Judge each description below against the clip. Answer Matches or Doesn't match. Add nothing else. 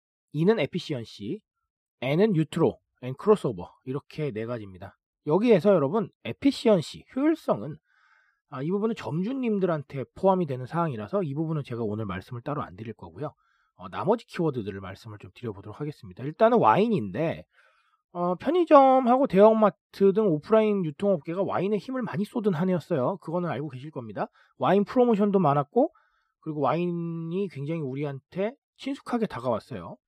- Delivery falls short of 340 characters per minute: Doesn't match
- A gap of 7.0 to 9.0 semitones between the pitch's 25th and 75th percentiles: Matches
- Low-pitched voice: Doesn't match